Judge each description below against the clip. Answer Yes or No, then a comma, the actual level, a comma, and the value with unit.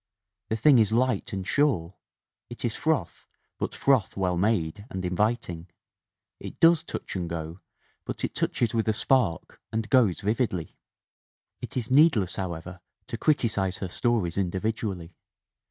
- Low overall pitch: Yes, low, 105 Hz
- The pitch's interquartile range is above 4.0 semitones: Yes, average, 5.0 semitones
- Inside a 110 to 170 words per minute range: Yes, average, 150 wpm